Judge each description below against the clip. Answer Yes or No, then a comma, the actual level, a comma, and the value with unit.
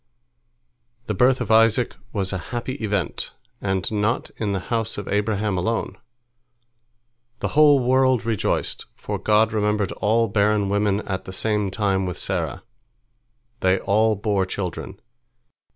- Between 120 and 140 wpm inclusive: Yes, slow, 135 wpm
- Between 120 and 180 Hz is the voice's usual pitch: No, low, 105 Hz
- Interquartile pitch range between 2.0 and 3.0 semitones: Yes, narrow, 2.5 semitones